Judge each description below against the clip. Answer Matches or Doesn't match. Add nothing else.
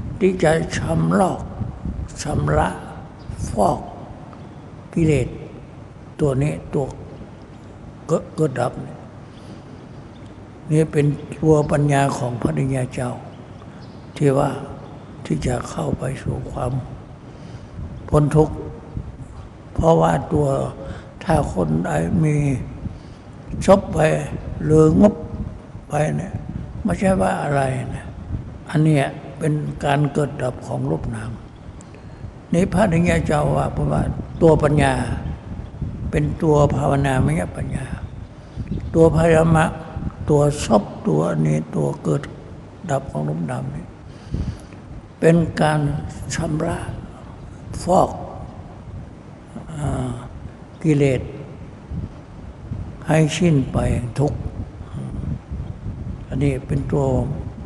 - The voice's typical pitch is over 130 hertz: Matches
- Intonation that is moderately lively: Matches